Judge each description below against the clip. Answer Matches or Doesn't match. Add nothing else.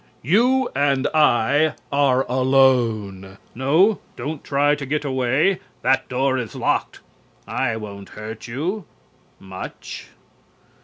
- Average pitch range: Matches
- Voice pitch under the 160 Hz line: Matches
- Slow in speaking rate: Matches